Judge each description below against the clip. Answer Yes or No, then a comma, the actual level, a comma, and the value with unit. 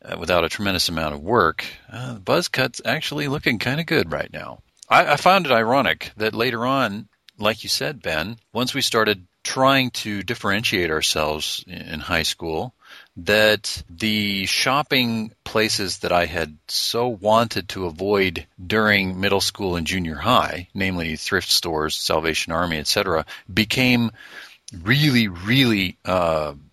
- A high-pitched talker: No, low, 105 Hz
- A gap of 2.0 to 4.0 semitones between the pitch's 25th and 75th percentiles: No, average, 5.1 semitones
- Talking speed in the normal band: Yes, average, 150 wpm